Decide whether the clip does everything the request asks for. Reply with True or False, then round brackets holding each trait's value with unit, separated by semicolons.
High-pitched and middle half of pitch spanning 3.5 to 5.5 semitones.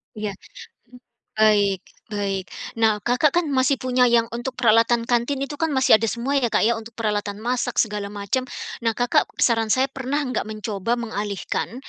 False (235 Hz; 3.1 semitones)